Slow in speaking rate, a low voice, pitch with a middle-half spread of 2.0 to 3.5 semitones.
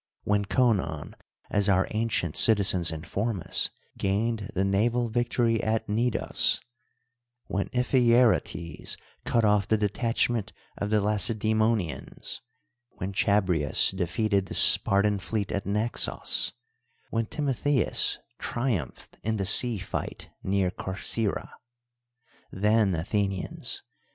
Yes: slow, 105 wpm; low, 105 Hz; average, 2.9 semitones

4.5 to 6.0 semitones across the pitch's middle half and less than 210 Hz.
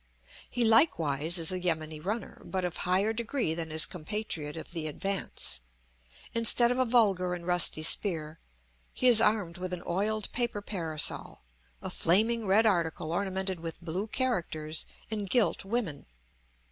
Yes: average, 5.0 semitones; medium, 185 Hz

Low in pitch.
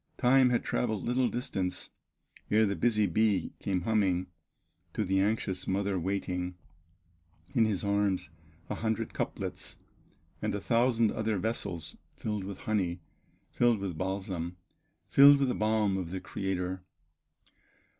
Yes: low, 100 Hz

